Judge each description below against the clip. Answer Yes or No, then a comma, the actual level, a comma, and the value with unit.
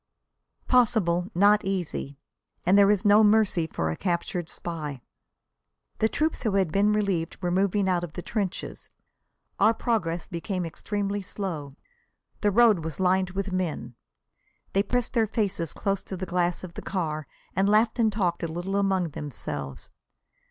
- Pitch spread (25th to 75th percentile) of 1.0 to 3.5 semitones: Yes, average, 3.2 semitones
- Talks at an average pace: Yes, average, 160 wpm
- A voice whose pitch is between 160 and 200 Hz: Yes, high, 190 Hz